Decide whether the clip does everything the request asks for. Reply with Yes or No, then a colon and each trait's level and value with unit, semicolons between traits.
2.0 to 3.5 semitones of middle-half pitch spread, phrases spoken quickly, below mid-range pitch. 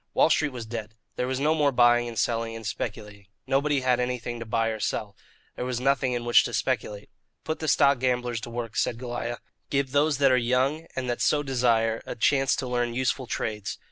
Yes: average, 2.8 semitones; fast, 215 wpm; low, 125 Hz